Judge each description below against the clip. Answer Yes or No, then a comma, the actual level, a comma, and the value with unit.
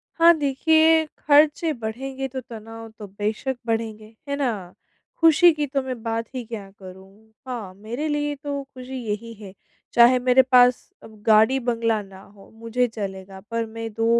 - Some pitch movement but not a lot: Yes, average, 3.7 semitones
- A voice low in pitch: No, high, 235 Hz